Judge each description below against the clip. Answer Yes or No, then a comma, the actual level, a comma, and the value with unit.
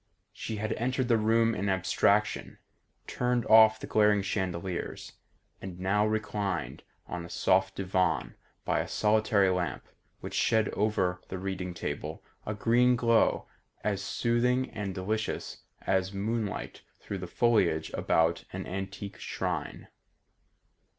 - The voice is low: Yes, low, 100 Hz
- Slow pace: Yes, slow, 130 wpm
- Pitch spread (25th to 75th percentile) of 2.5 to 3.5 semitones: Yes, average, 2.9 semitones